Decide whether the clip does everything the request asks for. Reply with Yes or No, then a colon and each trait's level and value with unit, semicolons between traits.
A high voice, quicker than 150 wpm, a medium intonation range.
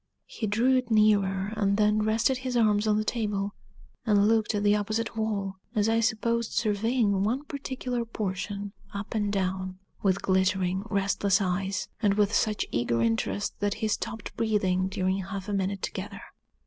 No: high, 205 Hz; average, 165 wpm; narrow, 2.1 semitones